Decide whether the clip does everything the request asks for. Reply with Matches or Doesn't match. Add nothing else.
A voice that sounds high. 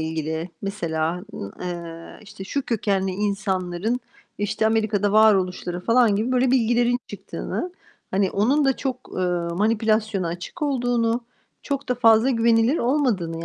Matches